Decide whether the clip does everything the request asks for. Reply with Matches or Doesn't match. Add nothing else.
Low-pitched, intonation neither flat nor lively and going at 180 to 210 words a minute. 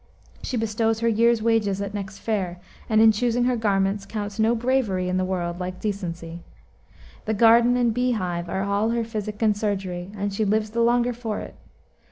Doesn't match